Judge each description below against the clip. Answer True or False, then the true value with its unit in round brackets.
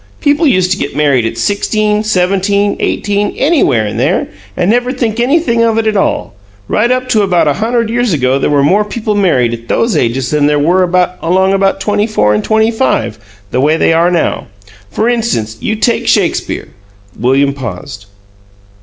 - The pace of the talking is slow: False (190 wpm)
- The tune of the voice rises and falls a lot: True (7.8 semitones)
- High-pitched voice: True (195 Hz)